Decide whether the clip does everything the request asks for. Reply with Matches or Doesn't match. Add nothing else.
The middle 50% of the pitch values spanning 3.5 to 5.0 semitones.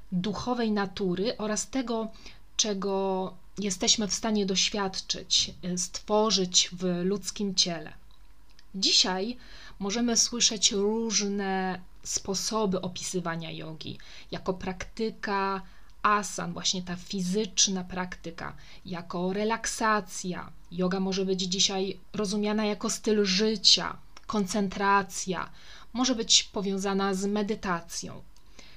Doesn't match